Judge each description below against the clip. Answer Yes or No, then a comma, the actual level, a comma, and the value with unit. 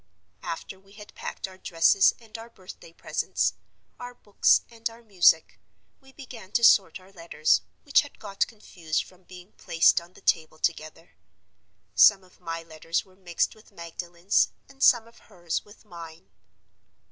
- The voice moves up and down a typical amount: Yes, average, 4.5 semitones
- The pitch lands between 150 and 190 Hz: Yes, medium, 185 Hz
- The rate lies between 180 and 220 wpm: No, average, 160 wpm